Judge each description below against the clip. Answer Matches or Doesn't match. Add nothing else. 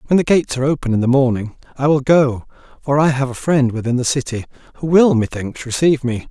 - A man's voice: Matches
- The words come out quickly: Matches